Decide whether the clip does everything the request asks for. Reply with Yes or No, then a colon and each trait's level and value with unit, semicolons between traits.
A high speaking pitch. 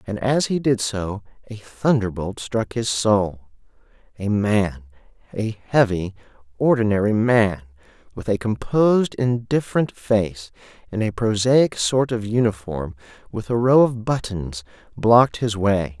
No: low, 110 Hz